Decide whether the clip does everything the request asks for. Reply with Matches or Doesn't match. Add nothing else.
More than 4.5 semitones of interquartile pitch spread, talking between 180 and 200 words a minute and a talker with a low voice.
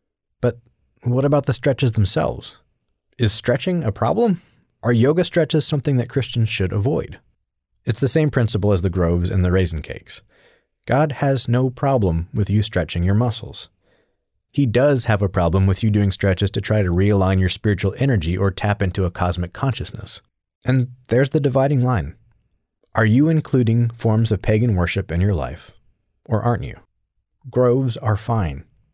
Doesn't match